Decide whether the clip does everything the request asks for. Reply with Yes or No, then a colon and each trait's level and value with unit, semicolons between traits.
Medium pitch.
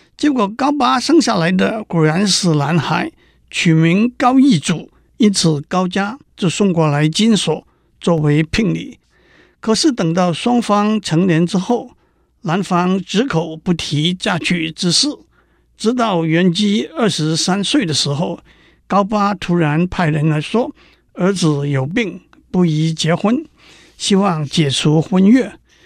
Yes: medium, 180 Hz